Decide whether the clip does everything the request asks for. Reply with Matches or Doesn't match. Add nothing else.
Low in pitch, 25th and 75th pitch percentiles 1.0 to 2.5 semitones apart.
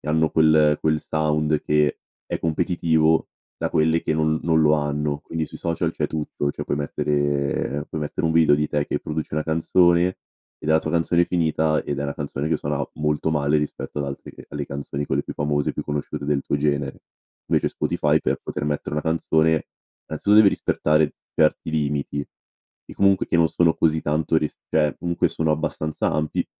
Matches